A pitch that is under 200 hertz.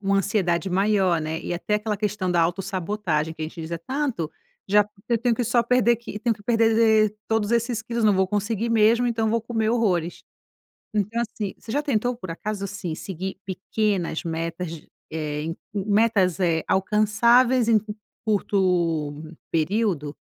No: high, 205 Hz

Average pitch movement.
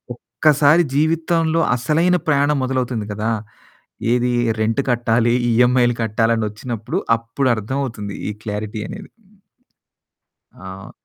Yes: average, 4.3 semitones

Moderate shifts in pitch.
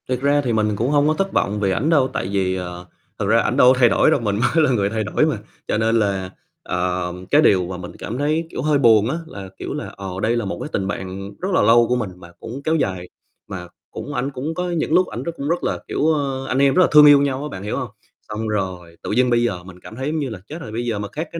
No: wide, 6.6 semitones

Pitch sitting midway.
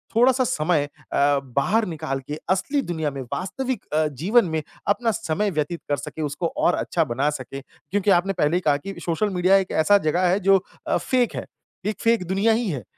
Yes: medium, 180 Hz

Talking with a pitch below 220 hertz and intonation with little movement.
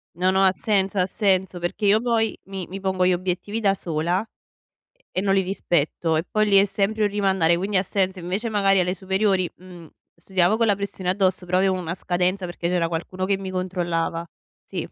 Yes: high, 190 Hz; narrow, 1.7 semitones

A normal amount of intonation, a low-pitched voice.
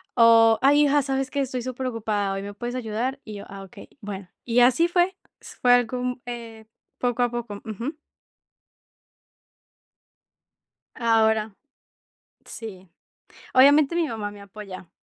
No: average, 3.5 semitones; high, 235 Hz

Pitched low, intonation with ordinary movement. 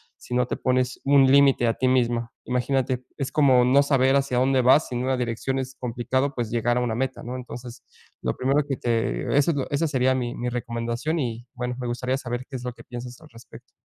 No: low, 125 Hz; narrow, 1.8 semitones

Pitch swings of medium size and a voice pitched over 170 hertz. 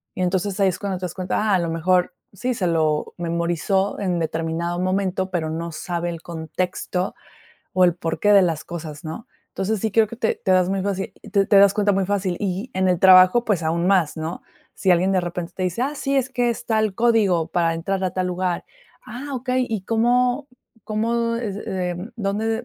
Yes: average, 3.6 semitones; medium, 185 Hz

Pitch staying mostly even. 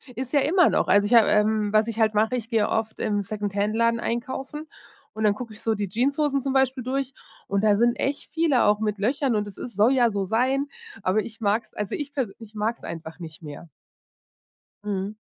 No: average, 3.8 semitones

